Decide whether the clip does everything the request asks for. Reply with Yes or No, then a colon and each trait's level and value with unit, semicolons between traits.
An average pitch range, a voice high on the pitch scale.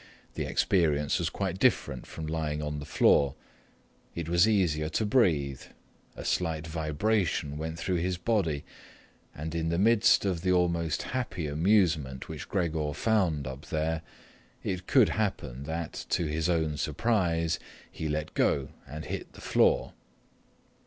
No: average, 3.3 semitones; very low, 80 Hz